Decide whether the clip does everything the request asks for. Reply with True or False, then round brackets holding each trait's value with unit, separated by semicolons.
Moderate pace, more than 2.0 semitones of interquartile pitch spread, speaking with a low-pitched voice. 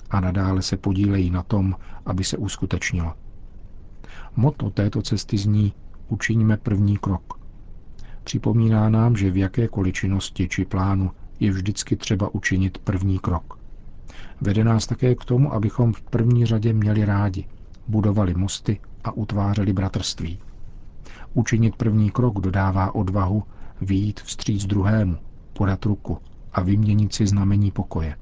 True (130 wpm; 2.4 semitones; 100 Hz)